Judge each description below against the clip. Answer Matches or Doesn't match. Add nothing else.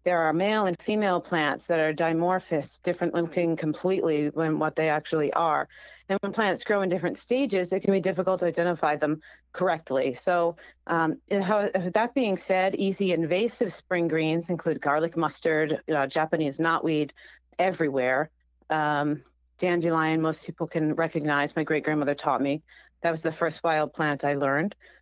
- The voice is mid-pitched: Matches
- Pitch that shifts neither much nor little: Matches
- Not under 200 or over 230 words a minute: Doesn't match